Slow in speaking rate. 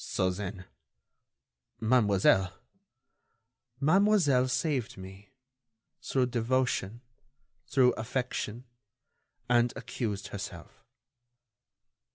Yes: slow, 65 wpm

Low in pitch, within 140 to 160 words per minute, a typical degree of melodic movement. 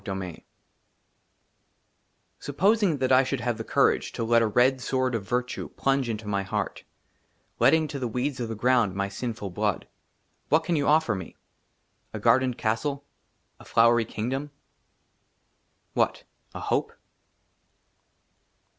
Yes: low, 125 Hz; average, 145 wpm; average, 3.8 semitones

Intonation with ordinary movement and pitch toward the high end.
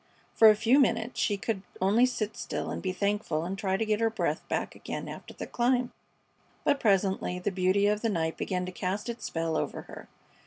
Yes: average, 3.4 semitones; high, 205 Hz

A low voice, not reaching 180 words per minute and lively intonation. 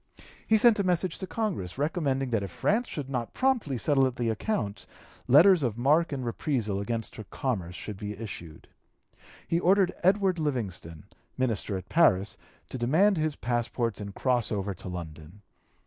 Yes: low, 125 Hz; average, 165 wpm; wide, 8.4 semitones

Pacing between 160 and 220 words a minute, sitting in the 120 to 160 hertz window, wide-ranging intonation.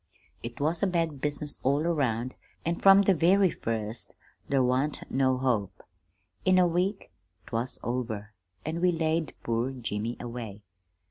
No: average, 145 wpm; low, 135 Hz; wide, 6.0 semitones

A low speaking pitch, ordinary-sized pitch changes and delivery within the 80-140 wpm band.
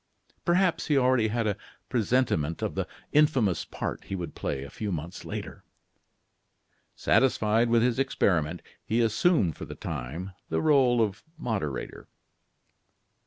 No: low, 115 Hz; wide, 6.2 semitones; slow, 135 wpm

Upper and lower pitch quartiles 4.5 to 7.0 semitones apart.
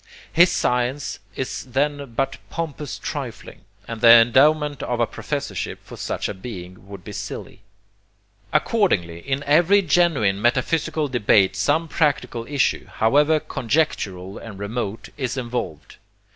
Yes: wide, 5.6 semitones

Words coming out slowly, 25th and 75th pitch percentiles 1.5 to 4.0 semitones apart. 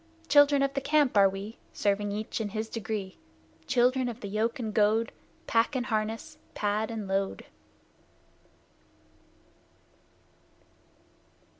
Yes: slow, 120 wpm; average, 3.3 semitones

